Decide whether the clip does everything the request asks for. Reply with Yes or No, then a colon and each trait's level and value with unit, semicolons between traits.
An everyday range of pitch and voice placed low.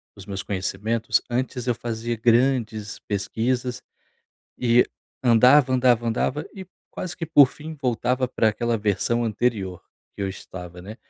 Yes: average, 3.1 semitones; low, 115 Hz